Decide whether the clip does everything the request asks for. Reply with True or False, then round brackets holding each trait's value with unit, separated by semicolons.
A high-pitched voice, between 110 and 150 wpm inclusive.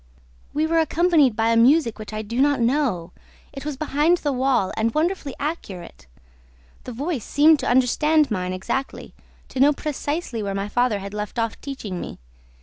False (260 Hz; 175 wpm)